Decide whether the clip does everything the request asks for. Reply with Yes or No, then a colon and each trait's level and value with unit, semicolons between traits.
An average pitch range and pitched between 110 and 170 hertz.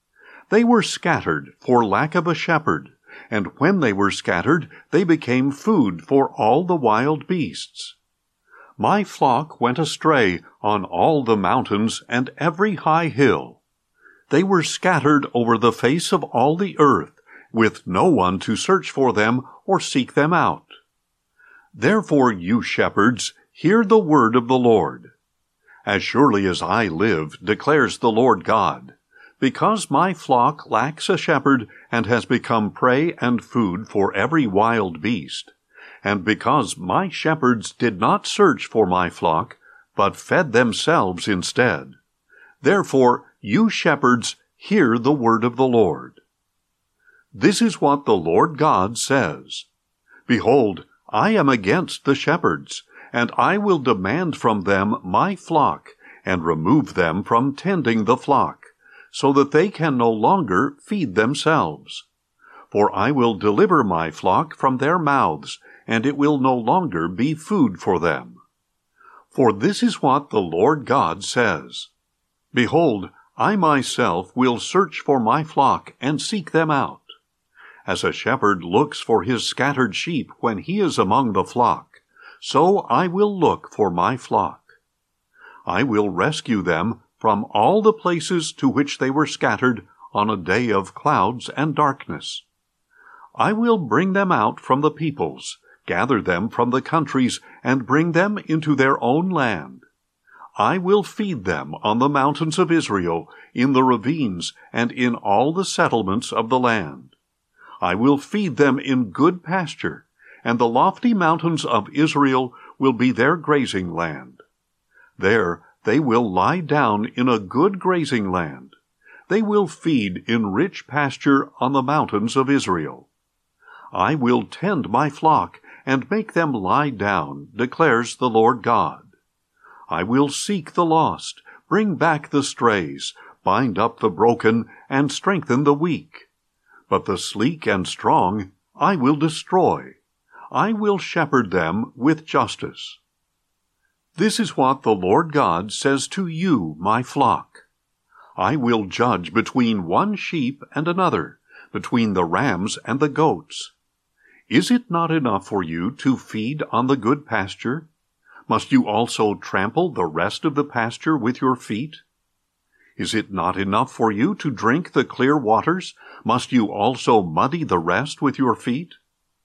No: wide, 6.8 semitones; medium, 140 Hz